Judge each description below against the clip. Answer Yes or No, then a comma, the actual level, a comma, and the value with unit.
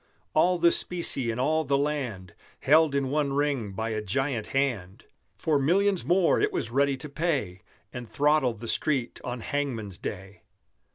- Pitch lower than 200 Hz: Yes, medium, 140 Hz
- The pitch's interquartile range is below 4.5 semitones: No, average, 4.9 semitones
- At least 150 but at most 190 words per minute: Yes, average, 165 wpm